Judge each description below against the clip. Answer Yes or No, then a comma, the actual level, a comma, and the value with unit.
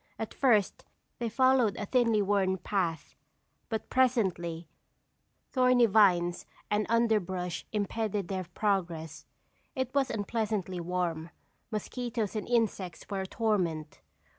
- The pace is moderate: No, slow, 115 wpm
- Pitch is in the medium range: No, high, 205 Hz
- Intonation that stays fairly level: No, average, 4.3 semitones